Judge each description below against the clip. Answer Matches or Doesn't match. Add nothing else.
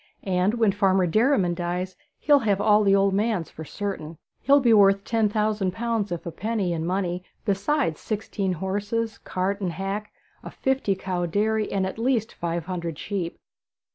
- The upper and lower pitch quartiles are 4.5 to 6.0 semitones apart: Doesn't match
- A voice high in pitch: Matches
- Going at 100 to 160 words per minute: Doesn't match